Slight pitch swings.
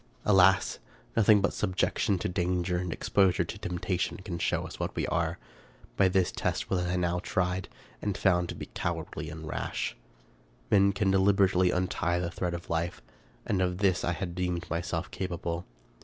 Yes: narrow, 1.7 semitones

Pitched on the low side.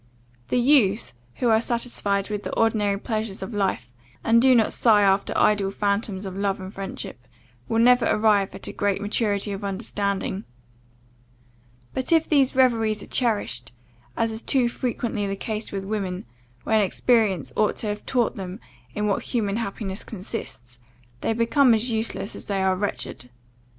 No: high, 210 Hz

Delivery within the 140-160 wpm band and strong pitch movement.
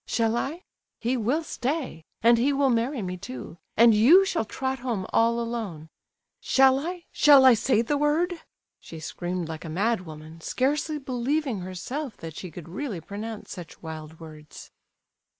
Yes: average, 155 wpm; wide, 7.5 semitones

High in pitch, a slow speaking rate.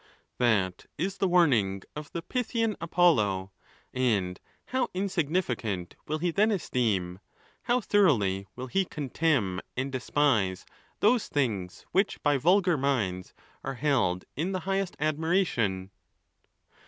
No: medium, 140 Hz; slow, 120 wpm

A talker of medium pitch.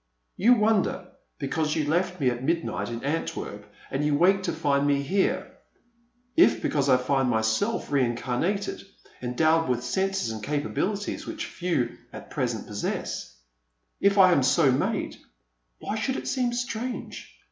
Yes: medium, 150 Hz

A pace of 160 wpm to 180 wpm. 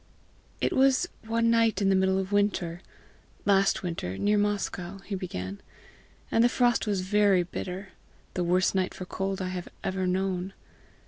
Yes: average, 165 wpm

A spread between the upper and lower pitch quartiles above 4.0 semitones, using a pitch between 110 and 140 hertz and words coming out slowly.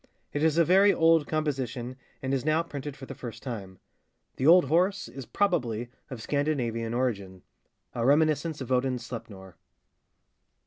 No: average, 4.9 semitones; low, 135 Hz; average, 145 wpm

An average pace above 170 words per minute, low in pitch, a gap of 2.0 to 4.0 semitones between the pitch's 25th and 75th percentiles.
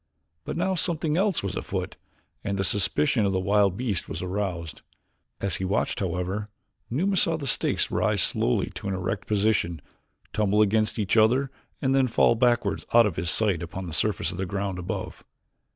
No: average, 185 wpm; low, 105 Hz; average, 4.4 semitones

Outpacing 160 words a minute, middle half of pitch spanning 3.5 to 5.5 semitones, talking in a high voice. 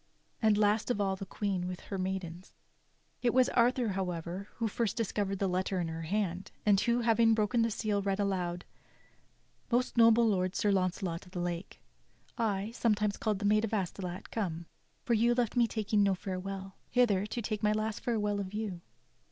No: average, 185 wpm; average, 2.9 semitones; high, 205 Hz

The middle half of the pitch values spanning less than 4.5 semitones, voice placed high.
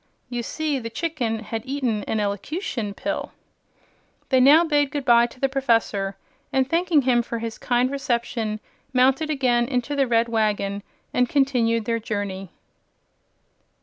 Yes: average, 3.5 semitones; high, 245 Hz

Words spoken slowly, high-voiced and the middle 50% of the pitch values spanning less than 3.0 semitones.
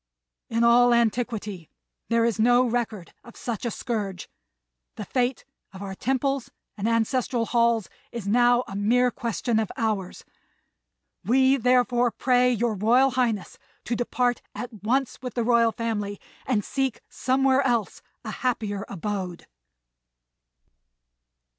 Yes: slow, 130 wpm; high, 235 Hz; narrow, 2.6 semitones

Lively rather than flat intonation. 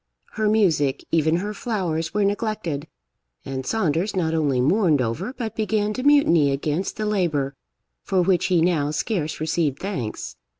Yes: wide, 5.9 semitones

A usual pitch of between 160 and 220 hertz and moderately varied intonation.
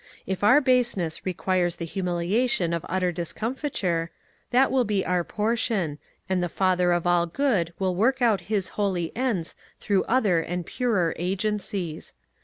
Yes: high, 190 Hz; average, 4.4 semitones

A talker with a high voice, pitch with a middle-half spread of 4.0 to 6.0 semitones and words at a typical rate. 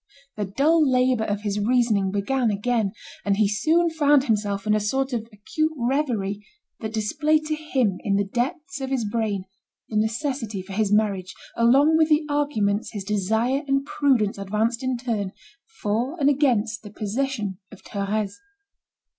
Yes: high, 225 Hz; average, 4.9 semitones; average, 165 wpm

